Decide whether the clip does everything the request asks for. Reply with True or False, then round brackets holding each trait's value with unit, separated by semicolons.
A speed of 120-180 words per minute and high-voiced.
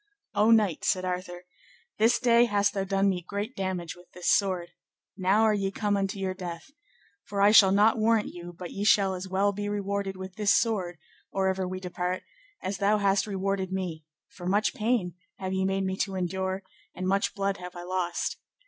False (200 wpm; 195 Hz)